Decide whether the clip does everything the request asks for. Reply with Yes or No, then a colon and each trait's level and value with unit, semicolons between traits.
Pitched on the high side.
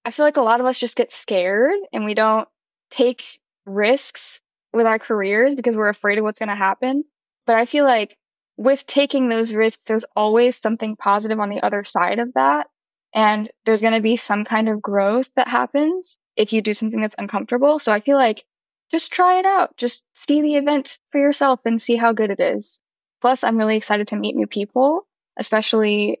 Yes: high, 225 Hz